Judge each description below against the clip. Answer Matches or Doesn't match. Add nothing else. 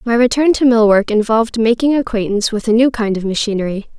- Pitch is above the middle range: Matches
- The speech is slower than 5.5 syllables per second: Doesn't match